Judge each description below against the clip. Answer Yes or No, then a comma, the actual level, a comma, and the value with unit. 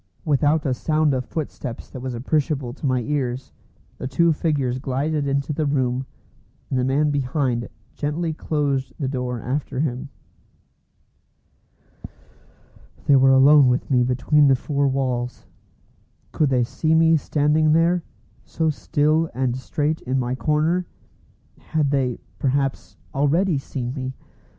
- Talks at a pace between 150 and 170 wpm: No, slow, 135 wpm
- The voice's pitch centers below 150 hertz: Yes, medium, 140 Hz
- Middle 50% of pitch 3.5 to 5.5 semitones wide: No, average, 2.8 semitones